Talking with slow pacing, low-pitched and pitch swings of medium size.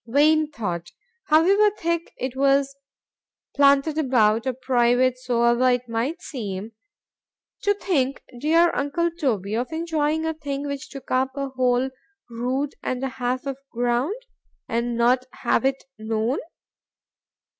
No: slow, 125 wpm; very high, 265 Hz; average, 3.8 semitones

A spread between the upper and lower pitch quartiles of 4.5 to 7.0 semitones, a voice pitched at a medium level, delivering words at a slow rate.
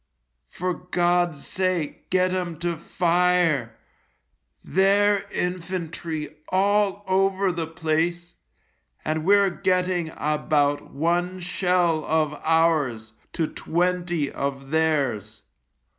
No: average, 2.8 semitones; medium, 175 Hz; slow, 95 wpm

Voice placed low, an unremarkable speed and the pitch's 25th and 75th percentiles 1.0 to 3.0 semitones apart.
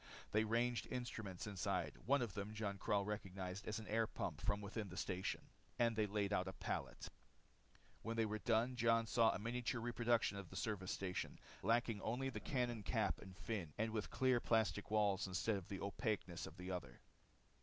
Yes: low, 110 Hz; average, 190 wpm; average, 2.7 semitones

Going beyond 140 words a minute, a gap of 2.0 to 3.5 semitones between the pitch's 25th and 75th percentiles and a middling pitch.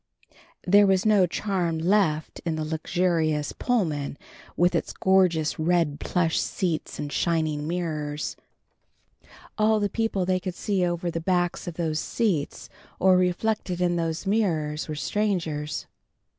No: slow, 135 wpm; average, 3.2 semitones; medium, 175 Hz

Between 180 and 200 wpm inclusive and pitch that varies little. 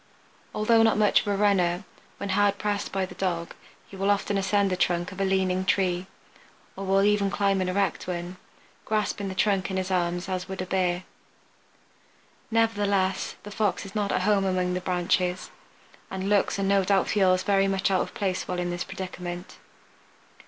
Yes: average, 190 wpm; narrow, 1.7 semitones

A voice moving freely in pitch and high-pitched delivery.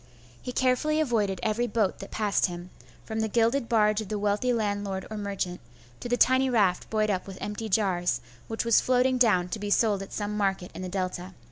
No: average, 3.2 semitones; high, 210 Hz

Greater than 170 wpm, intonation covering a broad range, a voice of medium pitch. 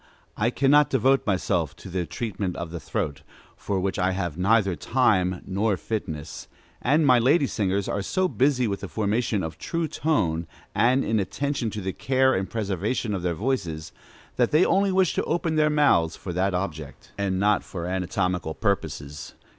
No: average, 180 wpm; wide, 6.2 semitones; low, 100 Hz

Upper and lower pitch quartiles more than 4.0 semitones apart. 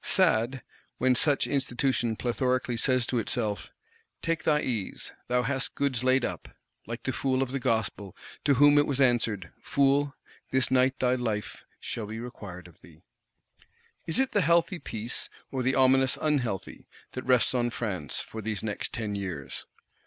No: average, 3.3 semitones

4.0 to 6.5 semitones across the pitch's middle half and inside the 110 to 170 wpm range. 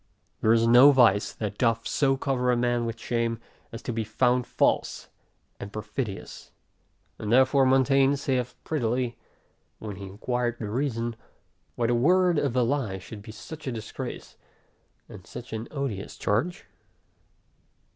No: average, 3.0 semitones; average, 150 wpm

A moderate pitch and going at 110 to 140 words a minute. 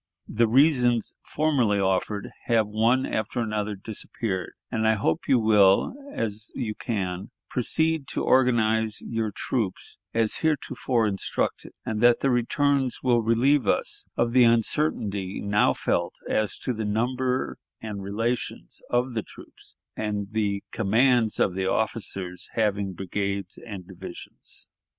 No: low, 110 Hz; slow, 135 wpm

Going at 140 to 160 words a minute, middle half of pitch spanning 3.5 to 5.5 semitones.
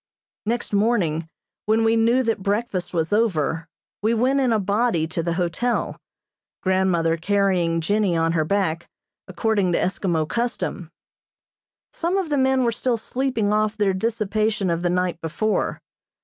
Yes: average, 150 wpm; average, 4.9 semitones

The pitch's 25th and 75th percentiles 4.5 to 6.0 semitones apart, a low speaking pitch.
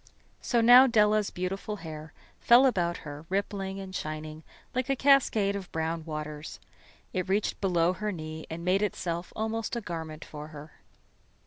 No: average, 4.9 semitones; medium, 185 Hz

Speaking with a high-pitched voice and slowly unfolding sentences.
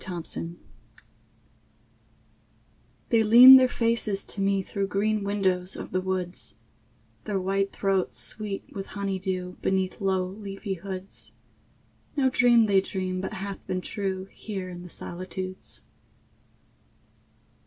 Yes: high, 195 Hz; slow, 125 wpm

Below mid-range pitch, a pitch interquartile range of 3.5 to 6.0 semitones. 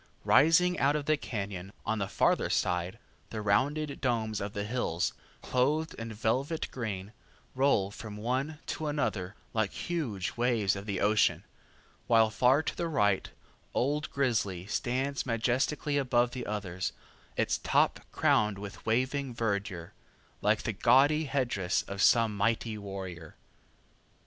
Yes: low, 115 Hz; average, 5.3 semitones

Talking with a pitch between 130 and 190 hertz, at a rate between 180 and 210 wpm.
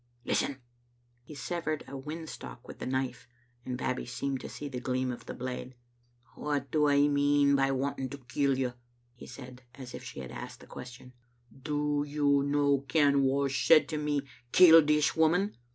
Yes: medium, 140 Hz; average, 185 wpm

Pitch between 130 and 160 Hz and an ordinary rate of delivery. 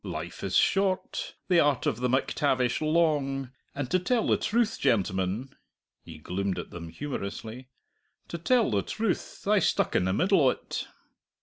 Yes: low, 135 Hz; average, 160 wpm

